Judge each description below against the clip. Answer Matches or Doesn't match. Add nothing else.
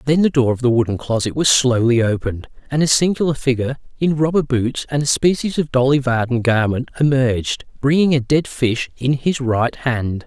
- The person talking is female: Doesn't match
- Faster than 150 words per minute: Matches